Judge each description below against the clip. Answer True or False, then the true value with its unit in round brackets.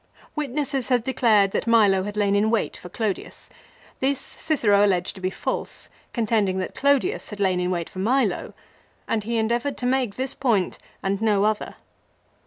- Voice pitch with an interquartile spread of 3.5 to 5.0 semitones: True (4.5 semitones)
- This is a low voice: False (220 Hz)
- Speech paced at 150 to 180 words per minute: True (175 wpm)